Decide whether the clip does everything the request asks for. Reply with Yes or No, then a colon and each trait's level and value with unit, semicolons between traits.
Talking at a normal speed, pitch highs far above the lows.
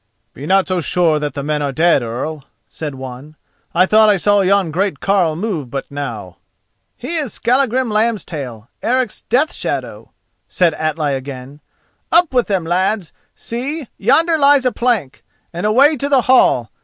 Yes: average, 155 wpm; wide, 8.5 semitones